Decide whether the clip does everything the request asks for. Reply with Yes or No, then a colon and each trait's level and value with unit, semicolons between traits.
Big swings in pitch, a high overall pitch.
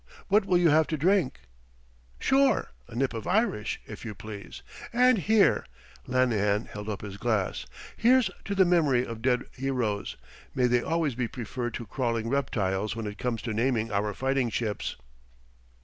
No: wide, 6.6 semitones; low, 125 Hz